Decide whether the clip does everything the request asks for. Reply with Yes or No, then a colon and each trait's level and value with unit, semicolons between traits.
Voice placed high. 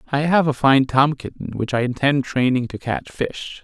No: low, 135 Hz